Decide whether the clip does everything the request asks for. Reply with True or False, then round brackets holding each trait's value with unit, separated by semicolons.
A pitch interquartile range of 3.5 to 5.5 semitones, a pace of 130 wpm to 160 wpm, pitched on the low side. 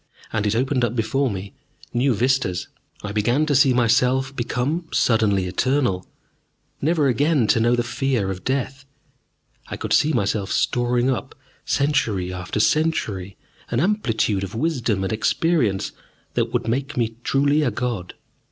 True (4.6 semitones; 150 wpm; 120 Hz)